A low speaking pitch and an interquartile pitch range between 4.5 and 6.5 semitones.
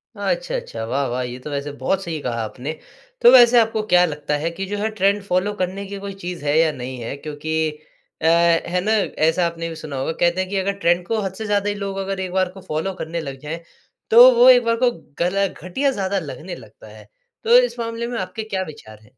No: medium, 185 Hz; average, 4.8 semitones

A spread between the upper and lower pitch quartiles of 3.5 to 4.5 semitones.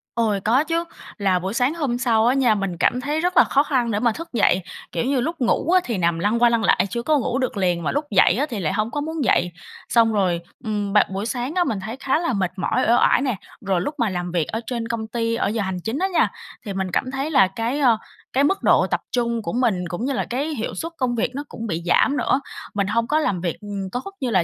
No: average, 5.3 semitones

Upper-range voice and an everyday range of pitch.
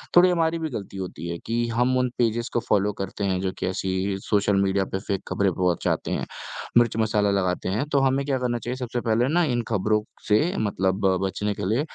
No: low, 105 Hz; average, 4.1 semitones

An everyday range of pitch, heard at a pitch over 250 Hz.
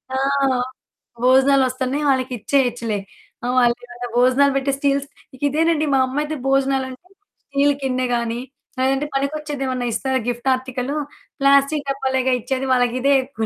No: narrow, 1.7 semitones; very high, 265 Hz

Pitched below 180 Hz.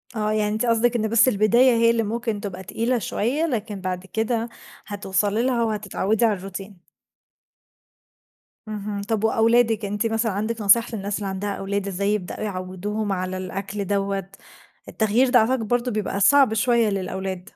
No: high, 210 Hz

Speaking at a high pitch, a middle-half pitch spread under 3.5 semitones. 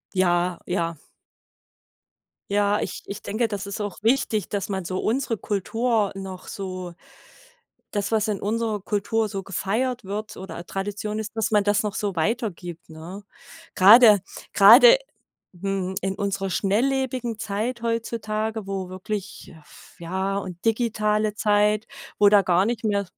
Yes: high, 205 Hz; narrow, 2.4 semitones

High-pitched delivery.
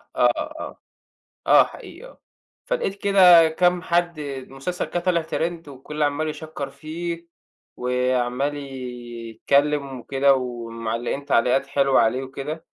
No: medium, 140 Hz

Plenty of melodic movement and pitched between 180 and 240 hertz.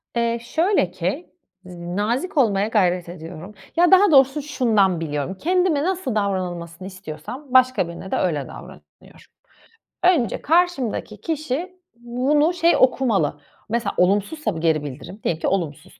Yes: wide, 8.9 semitones; high, 220 Hz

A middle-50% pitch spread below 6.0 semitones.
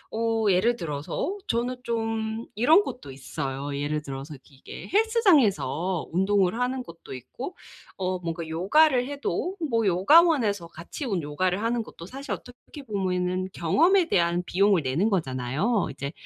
No: wide, 6.9 semitones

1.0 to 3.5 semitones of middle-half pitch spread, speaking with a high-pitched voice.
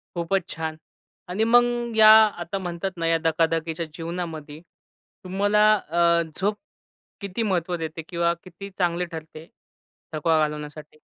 No: average, 3.2 semitones; medium, 170 Hz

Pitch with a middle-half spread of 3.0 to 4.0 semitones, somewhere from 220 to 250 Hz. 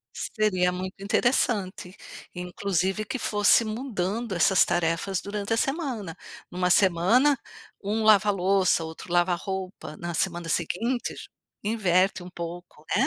No: average, 3.3 semitones; high, 190 Hz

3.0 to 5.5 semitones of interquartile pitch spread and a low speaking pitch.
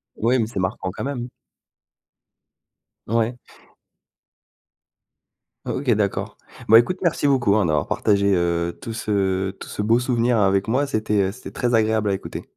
Yes: average, 3.5 semitones; low, 110 Hz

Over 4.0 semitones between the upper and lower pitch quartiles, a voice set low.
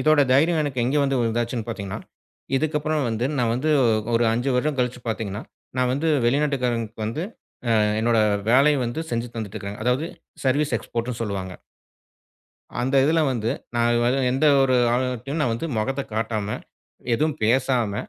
No: average, 3.3 semitones; low, 125 Hz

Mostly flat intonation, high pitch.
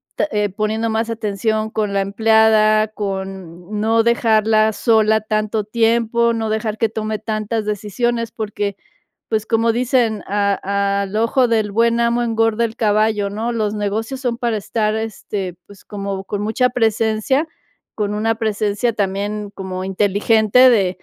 Yes: narrow, 1.7 semitones; high, 215 Hz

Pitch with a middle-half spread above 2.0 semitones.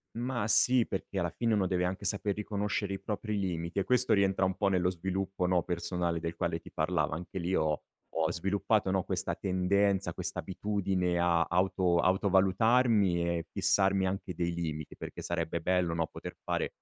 Yes: narrow, 2.5 semitones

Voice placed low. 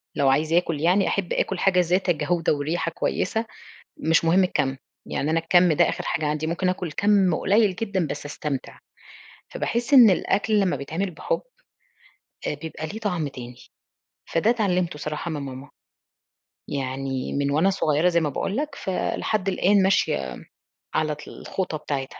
No: medium, 170 Hz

